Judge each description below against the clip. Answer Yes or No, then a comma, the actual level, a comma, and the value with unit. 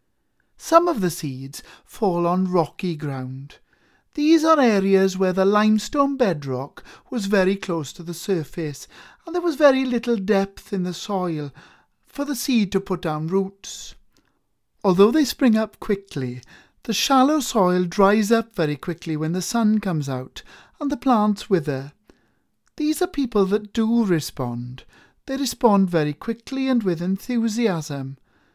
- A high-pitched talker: Yes, high, 195 Hz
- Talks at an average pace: Yes, average, 150 wpm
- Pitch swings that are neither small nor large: No, wide, 6.3 semitones